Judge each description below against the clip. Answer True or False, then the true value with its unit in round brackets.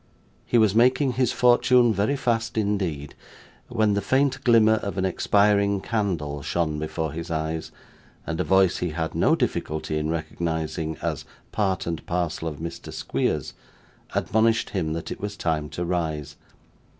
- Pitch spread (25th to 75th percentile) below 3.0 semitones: False (5.5 semitones)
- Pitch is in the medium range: False (95 Hz)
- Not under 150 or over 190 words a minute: True (155 wpm)